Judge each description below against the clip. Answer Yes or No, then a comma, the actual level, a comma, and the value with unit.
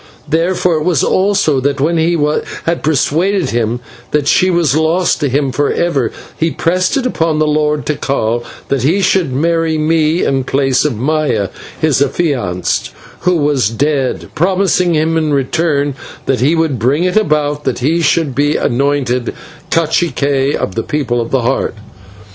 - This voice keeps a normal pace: Yes, average, 160 wpm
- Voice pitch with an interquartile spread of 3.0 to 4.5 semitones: Yes, average, 3.6 semitones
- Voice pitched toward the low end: No, medium, 150 Hz